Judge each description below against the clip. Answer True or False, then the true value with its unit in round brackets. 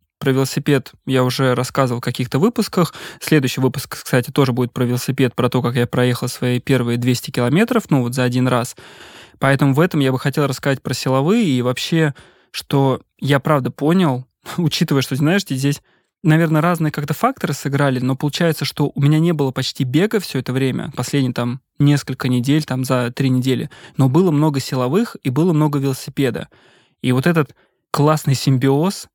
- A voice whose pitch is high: False (135 Hz)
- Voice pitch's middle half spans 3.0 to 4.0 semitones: True (3.3 semitones)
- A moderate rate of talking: False (175 wpm)